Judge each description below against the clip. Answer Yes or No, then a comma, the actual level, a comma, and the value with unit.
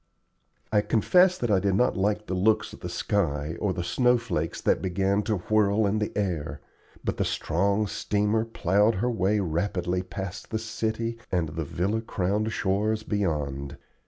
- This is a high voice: No, low, 100 Hz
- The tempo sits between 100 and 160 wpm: No, average, 175 wpm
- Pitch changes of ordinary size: Yes, average, 3.3 semitones